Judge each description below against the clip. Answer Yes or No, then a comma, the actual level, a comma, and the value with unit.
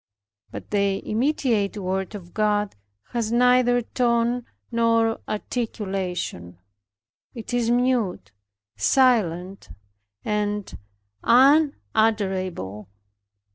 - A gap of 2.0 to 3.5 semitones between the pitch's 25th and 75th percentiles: No, average, 4.0 semitones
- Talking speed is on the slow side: Yes, slow, 75 wpm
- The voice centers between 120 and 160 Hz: No, high, 215 Hz